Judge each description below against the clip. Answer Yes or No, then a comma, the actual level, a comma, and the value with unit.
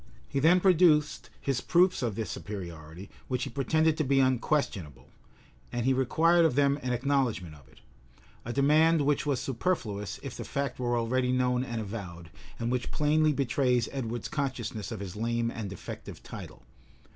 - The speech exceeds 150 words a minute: Yes, average, 170 wpm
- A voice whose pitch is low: Yes, low, 125 Hz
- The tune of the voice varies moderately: Yes, average, 4.1 semitones